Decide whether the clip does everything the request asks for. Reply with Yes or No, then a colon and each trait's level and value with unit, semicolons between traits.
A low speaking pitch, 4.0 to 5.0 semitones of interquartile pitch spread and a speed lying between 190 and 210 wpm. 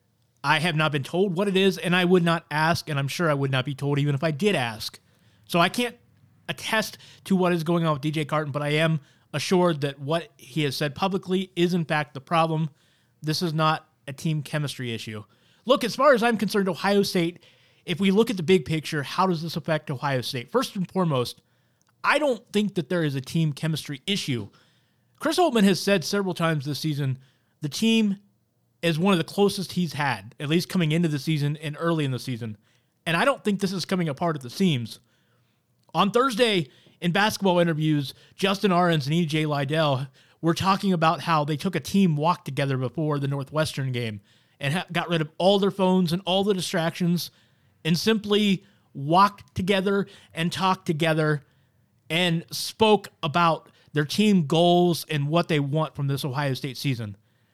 No: medium, 160 Hz; average, 4.6 semitones; average, 200 wpm